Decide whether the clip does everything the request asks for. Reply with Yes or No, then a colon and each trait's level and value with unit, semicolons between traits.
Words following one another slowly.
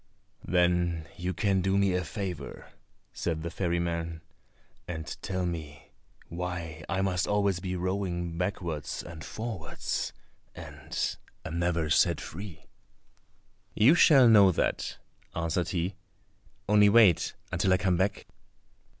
Yes: slow, 125 wpm